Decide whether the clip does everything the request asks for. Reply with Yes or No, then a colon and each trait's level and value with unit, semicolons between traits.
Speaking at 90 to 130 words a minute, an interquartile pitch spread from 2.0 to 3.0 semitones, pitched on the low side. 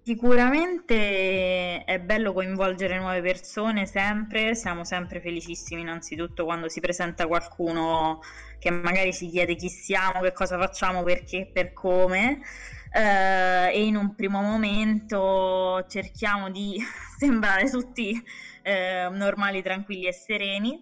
No: average, 125 wpm; narrow, 2.6 semitones; high, 190 Hz